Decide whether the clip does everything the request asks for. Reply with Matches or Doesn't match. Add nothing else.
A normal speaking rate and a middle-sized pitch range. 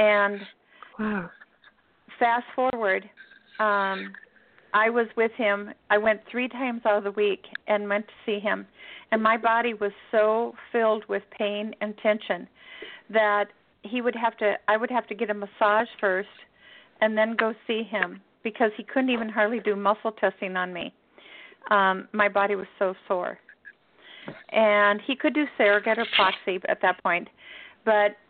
Doesn't match